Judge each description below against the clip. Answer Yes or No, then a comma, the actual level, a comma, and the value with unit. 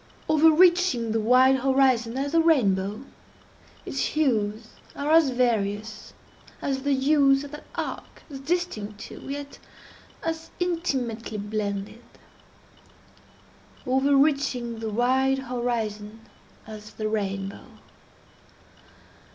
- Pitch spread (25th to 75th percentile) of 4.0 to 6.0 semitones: Yes, average, 4.7 semitones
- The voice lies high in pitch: Yes, very high, 255 Hz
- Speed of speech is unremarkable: No, slow, 95 wpm